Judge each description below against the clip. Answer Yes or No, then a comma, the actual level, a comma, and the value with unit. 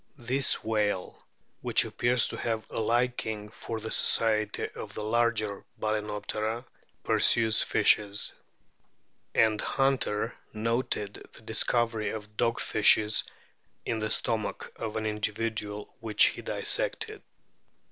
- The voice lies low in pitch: Yes, low, 110 Hz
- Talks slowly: Yes, slow, 115 wpm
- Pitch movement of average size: No, narrow, 1.5 semitones